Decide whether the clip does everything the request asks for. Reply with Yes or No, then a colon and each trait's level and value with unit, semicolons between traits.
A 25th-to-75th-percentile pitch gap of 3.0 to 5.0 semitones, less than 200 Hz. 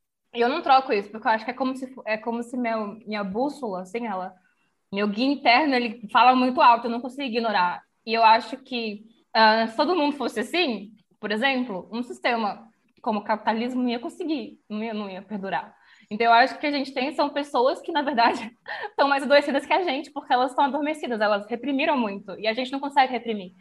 No: average, 4.2 semitones; high, 240 Hz